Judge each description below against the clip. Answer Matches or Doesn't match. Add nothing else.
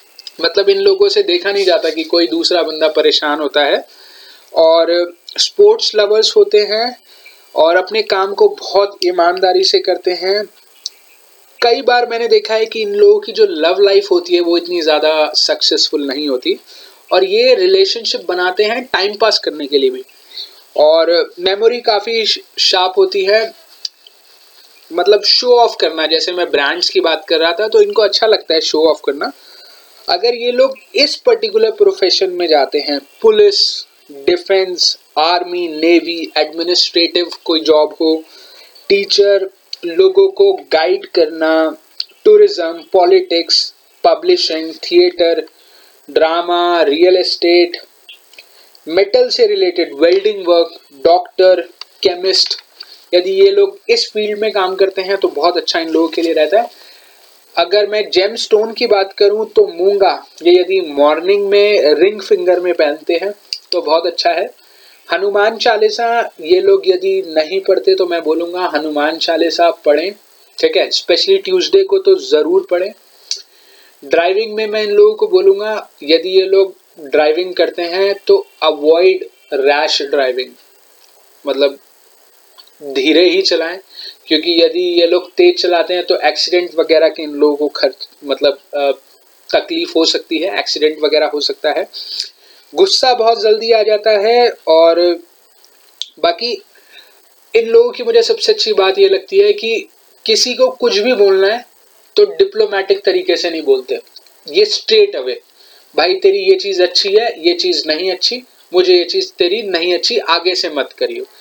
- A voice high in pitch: Matches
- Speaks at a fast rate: Doesn't match